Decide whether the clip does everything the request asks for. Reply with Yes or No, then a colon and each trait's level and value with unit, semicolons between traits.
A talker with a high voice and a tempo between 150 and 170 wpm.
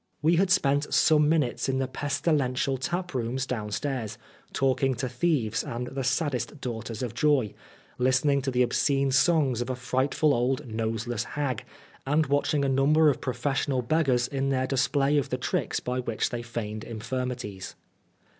No: low, 130 Hz; average, 155 wpm